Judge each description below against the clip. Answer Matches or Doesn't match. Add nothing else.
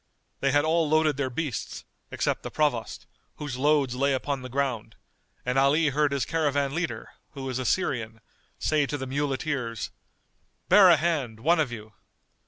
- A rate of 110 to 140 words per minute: Doesn't match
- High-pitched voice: Doesn't match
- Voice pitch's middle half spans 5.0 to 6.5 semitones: Doesn't match